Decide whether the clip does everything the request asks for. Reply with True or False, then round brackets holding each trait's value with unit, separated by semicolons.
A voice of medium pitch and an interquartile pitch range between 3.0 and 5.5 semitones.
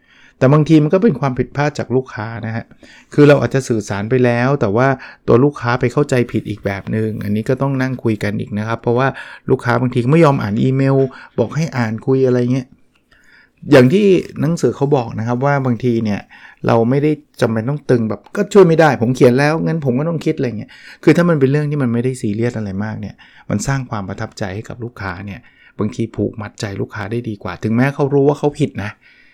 False (125 Hz; 4.2 semitones)